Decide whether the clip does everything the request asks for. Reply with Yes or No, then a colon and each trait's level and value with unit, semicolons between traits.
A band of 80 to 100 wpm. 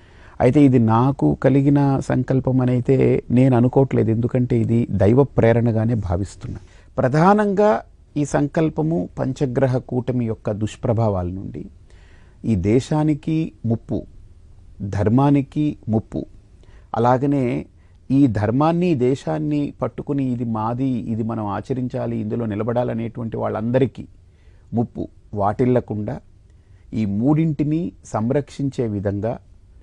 Yes: average, 90 wpm